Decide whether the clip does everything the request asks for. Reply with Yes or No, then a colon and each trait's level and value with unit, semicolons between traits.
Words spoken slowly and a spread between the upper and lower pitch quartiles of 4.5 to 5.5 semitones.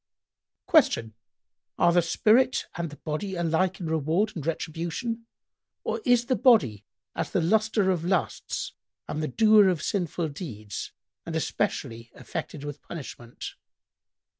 Yes: slow, 130 wpm; average, 5.2 semitones